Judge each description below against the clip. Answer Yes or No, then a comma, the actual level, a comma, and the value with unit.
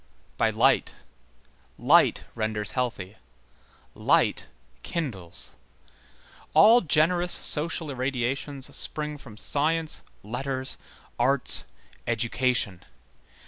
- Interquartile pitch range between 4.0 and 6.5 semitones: Yes, average, 4.7 semitones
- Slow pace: Yes, slow, 75 wpm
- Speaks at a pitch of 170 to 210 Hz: No, low, 130 Hz